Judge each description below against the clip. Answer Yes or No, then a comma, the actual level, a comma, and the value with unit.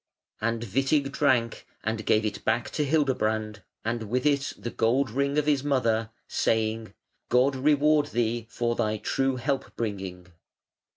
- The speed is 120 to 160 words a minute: Yes, average, 150 wpm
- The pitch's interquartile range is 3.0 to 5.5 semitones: Yes, average, 3.9 semitones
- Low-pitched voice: Yes, low, 120 Hz